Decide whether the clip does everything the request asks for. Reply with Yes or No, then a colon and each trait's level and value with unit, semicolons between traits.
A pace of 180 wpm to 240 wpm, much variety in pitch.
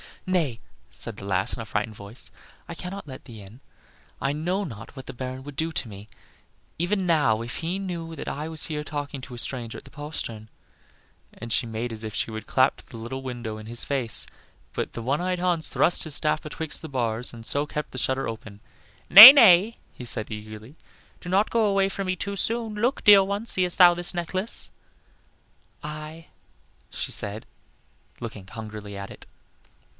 Yes: average, 195 wpm; wide, 7.7 semitones